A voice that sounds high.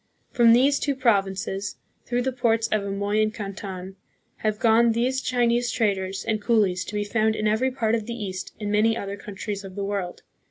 Yes: high, 215 Hz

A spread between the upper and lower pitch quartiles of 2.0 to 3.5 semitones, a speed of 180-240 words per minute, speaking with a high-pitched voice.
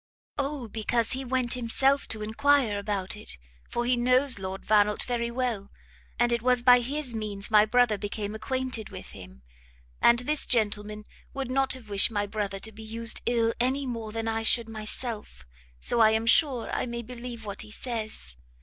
Yes: average, 2.8 semitones; average, 185 wpm; high, 230 Hz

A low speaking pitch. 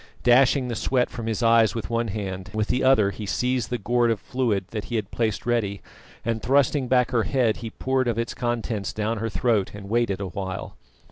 Yes: low, 115 Hz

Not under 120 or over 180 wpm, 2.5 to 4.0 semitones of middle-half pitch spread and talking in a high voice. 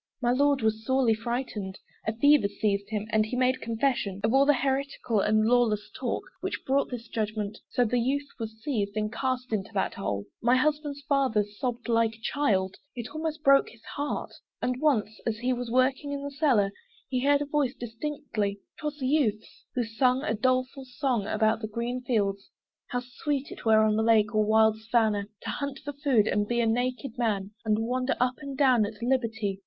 No: average, 195 wpm; average, 3.7 semitones; high, 240 Hz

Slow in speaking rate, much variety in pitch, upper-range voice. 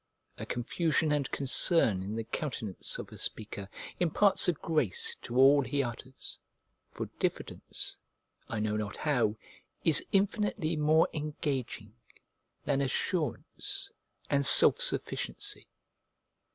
No: slow, 115 wpm; wide, 5.9 semitones; medium, 140 Hz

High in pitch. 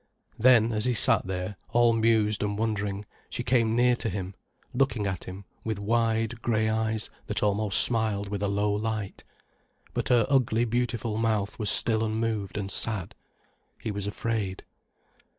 No: low, 110 Hz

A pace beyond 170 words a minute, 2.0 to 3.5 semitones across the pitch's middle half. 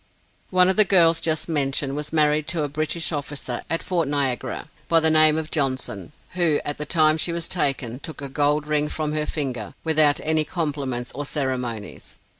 Yes: average, 190 wpm; narrow, 2.4 semitones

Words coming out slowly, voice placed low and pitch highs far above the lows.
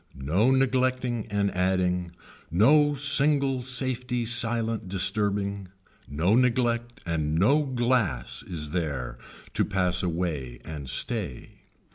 Yes: slow, 105 wpm; low, 105 Hz; wide, 6.6 semitones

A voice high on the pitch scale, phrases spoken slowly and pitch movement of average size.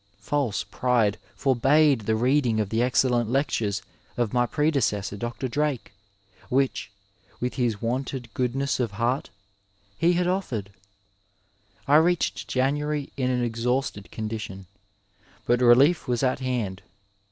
No: low, 125 Hz; slow, 125 wpm; average, 3.5 semitones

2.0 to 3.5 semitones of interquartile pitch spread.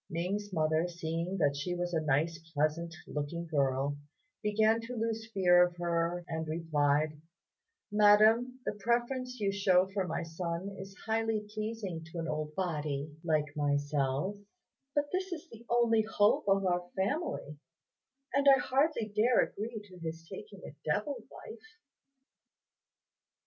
No: wide, 5.6 semitones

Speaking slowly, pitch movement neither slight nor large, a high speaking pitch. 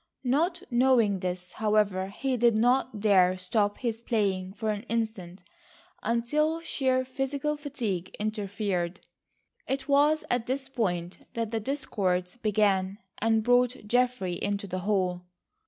Yes: slow, 130 wpm; average, 5.0 semitones; high, 220 Hz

